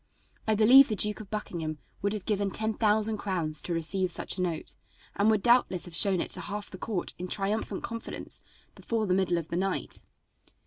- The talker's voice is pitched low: No, high, 200 Hz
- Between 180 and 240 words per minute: Yes, fast, 205 wpm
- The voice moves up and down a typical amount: Yes, average, 3.0 semitones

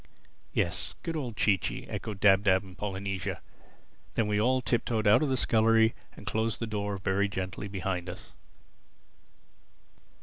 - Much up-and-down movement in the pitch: No, average, 2.7 semitones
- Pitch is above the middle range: No, low, 105 Hz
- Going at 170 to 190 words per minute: No, average, 155 wpm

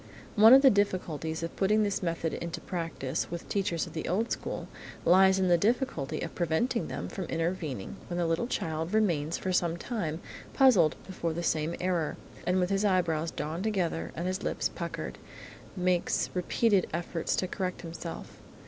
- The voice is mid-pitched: Yes, medium, 175 Hz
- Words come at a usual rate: Yes, average, 170 wpm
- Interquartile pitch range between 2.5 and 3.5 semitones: Yes, average, 3.0 semitones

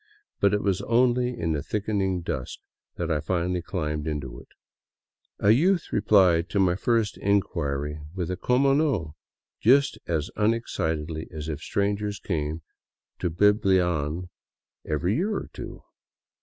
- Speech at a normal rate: Yes, average, 150 wpm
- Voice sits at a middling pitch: No, very low, 90 Hz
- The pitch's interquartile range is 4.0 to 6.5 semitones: Yes, average, 4.9 semitones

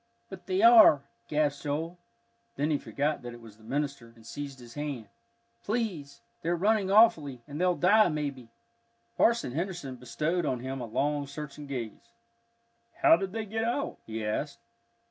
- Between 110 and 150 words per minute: No, average, 165 wpm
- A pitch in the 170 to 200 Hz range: No, medium, 150 Hz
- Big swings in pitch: Yes, wide, 6.0 semitones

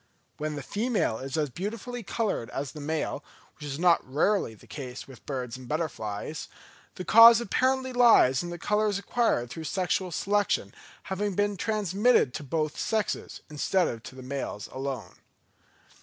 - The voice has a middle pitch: Yes, medium, 165 Hz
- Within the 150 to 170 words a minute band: Yes, average, 160 wpm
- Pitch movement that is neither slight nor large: No, wide, 7.4 semitones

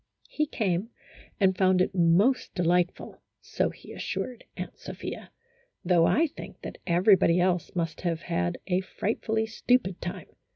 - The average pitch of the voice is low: No, medium, 185 Hz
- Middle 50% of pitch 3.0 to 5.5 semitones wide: Yes, average, 4.1 semitones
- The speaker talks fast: No, average, 150 wpm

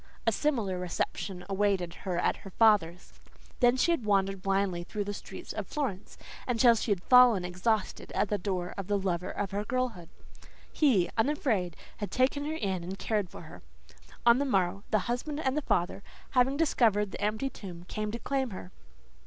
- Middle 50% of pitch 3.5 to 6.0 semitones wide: Yes, average, 4.9 semitones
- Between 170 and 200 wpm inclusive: Yes, average, 180 wpm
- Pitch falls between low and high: No, high, 205 Hz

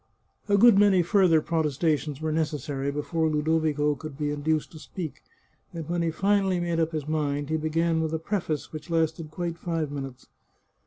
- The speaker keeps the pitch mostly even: Yes, narrow, 2.1 semitones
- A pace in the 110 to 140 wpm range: No, average, 180 wpm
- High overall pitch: No, medium, 160 Hz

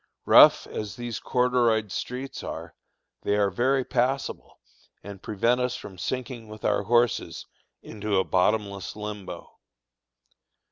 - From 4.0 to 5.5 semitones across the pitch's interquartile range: No, average, 3.4 semitones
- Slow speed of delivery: Yes, slow, 125 wpm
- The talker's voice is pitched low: Yes, low, 110 Hz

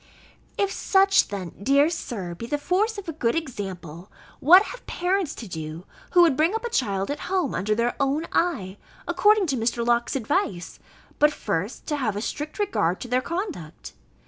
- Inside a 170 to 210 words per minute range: Yes, average, 185 wpm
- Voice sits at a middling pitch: No, very high, 275 Hz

